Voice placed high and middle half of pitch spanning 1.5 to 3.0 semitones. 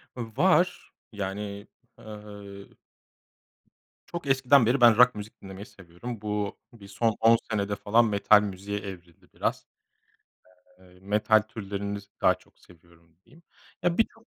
No: low, 105 Hz; average, 2.7 semitones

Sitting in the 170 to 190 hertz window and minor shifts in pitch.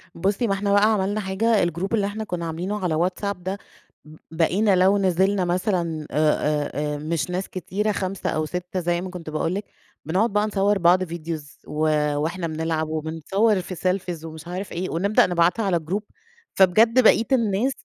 No: medium, 185 Hz; average, 3.5 semitones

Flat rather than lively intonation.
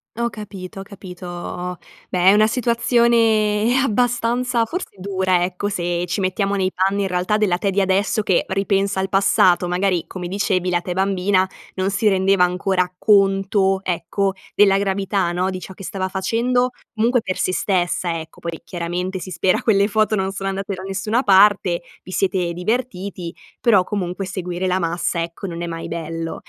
Yes: narrow, 2.2 semitones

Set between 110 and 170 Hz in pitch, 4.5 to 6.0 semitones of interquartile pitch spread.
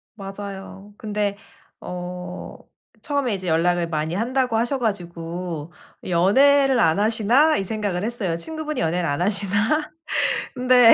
No: high, 200 Hz; average, 5.2 semitones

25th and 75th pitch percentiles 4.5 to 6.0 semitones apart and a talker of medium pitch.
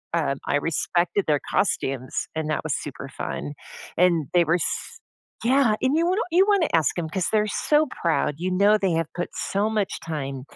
Yes: wide, 5.5 semitones; medium, 175 Hz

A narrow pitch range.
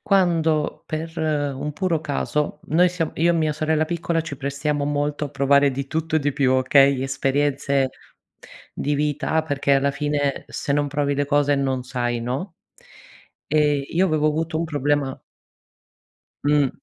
Yes: narrow, 2.1 semitones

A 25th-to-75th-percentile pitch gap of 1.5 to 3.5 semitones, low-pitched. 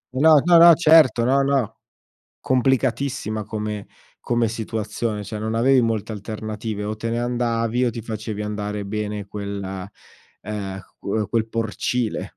Yes: narrow, 2.6 semitones; low, 110 Hz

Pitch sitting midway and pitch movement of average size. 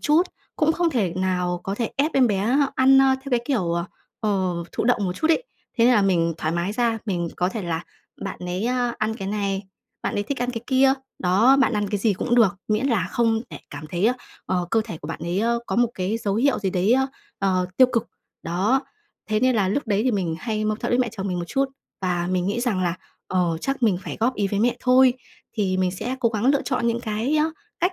No: high, 215 Hz; average, 5.0 semitones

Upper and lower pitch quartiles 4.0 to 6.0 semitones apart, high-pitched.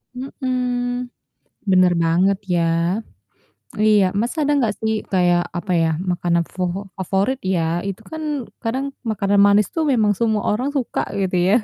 Yes: average, 5.0 semitones; high, 205 Hz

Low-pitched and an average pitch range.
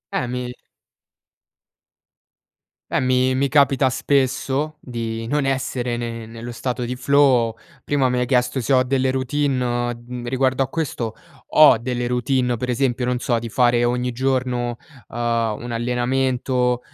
No: low, 125 Hz; narrow, 1.6 semitones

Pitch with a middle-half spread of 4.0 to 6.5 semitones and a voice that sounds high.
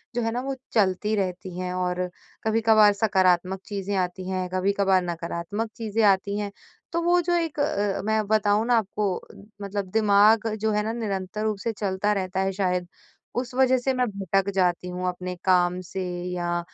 No: average, 2.9 semitones; high, 200 Hz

